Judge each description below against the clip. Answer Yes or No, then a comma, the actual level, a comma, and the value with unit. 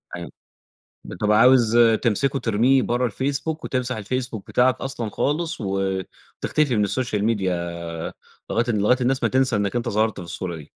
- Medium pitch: No, low, 120 Hz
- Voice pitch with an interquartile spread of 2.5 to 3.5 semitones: No, average, 4.0 semitones